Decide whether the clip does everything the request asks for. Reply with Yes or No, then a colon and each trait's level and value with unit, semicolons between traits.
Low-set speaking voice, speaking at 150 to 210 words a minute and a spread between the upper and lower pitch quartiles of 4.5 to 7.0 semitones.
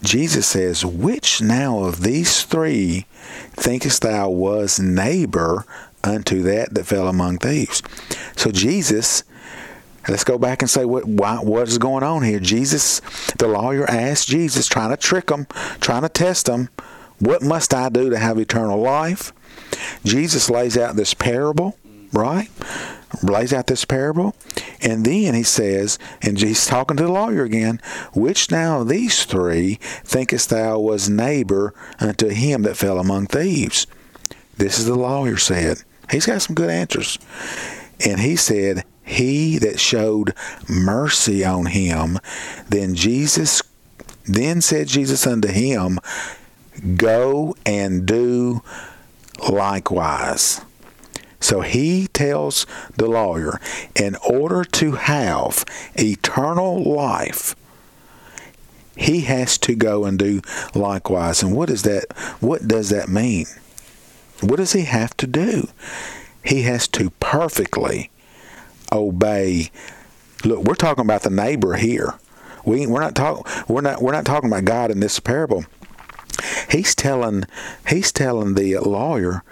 No: low, 115 Hz; slow, 135 wpm; wide, 5.4 semitones